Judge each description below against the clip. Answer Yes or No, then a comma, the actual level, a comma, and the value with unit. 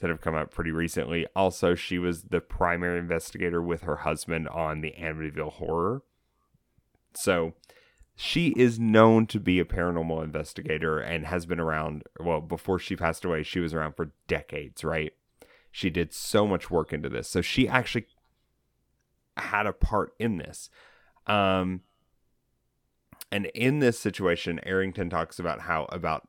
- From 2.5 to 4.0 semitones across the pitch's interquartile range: Yes, average, 3.0 semitones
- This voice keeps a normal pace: Yes, average, 155 wpm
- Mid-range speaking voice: No, very low, 85 Hz